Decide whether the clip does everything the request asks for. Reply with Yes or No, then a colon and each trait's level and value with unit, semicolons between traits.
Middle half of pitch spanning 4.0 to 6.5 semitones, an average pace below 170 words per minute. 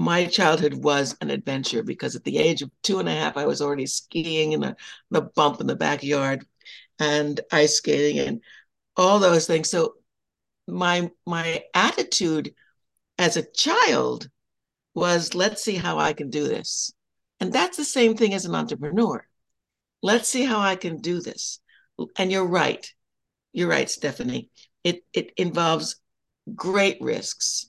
Yes: average, 4.6 semitones; average, 160 wpm